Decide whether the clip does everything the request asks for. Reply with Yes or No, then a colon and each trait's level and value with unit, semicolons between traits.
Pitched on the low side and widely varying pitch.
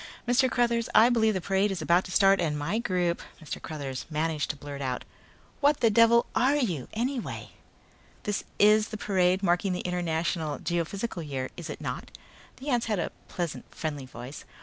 No: medium, 180 Hz; wide, 6.1 semitones